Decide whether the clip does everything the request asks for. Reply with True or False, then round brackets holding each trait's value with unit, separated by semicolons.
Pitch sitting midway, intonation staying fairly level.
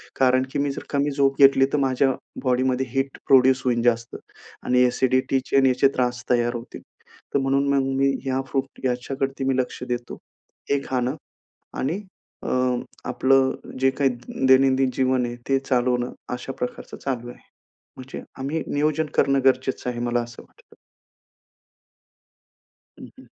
False (130 Hz; 1.6 semitones)